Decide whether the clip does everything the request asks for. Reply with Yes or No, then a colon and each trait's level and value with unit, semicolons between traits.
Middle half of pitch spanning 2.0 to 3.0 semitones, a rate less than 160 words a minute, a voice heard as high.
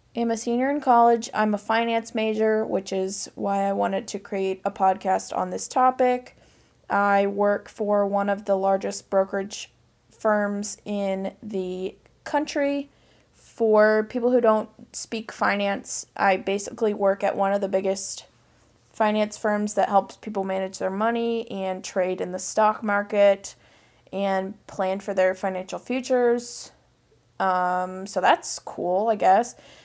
Yes: narrow, 2.4 semitones; average, 145 wpm; high, 200 Hz